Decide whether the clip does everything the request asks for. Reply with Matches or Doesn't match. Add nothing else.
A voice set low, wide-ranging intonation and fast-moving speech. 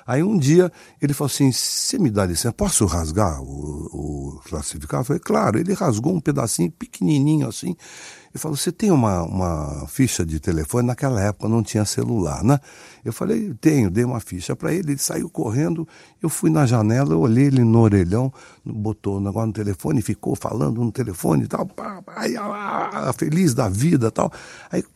Matches